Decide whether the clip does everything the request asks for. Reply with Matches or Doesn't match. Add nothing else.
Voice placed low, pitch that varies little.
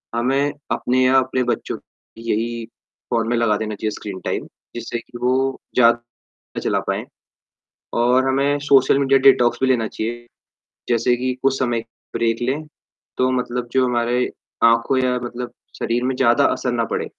Matches